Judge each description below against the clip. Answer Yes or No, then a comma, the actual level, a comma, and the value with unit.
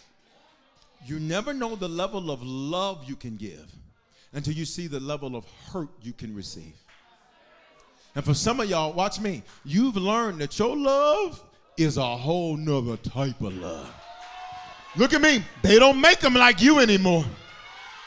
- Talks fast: No, average, 165 wpm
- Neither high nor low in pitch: Yes, medium, 170 Hz